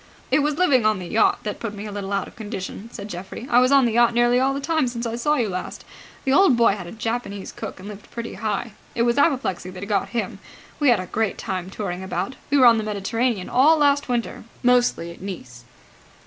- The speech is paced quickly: Yes, fast, 240 wpm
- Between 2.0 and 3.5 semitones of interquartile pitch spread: No, average, 4.1 semitones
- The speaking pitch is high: Yes, high, 230 Hz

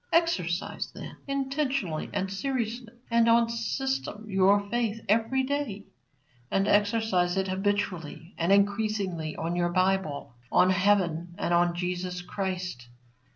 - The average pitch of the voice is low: No, high, 195 Hz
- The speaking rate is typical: No, slow, 120 wpm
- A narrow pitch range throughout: No, average, 4.3 semitones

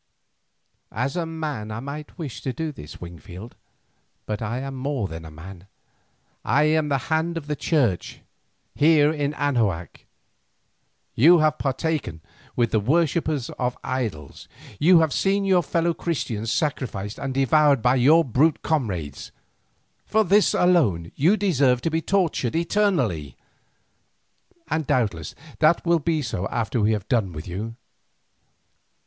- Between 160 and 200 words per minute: No, average, 140 wpm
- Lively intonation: Yes, wide, 6.8 semitones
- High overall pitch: No, low, 135 Hz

